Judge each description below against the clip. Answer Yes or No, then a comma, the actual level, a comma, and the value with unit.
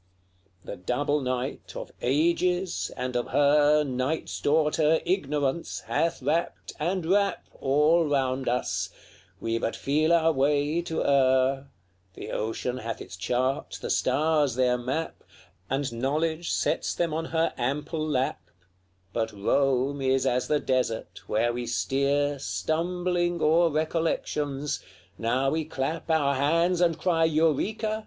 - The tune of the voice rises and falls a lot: No, average, 3.8 semitones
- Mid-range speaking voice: Yes, medium, 145 Hz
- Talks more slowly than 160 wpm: Yes, slow, 135 wpm